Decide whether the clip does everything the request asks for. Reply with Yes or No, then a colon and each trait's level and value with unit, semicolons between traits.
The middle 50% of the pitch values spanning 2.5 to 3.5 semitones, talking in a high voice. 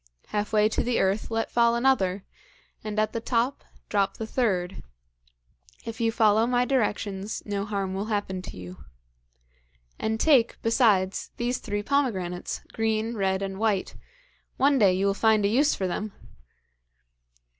Yes: average, 3.0 semitones; high, 215 Hz